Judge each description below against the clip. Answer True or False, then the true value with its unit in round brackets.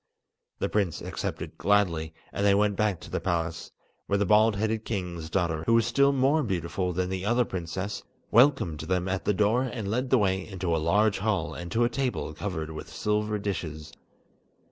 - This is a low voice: True (100 Hz)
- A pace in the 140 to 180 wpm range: False (190 wpm)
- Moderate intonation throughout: True (4.1 semitones)